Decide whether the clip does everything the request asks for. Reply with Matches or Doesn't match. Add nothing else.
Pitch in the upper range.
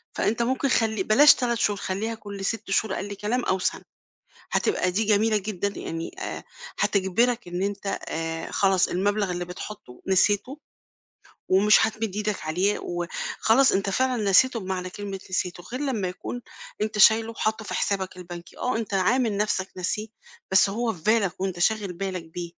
Matches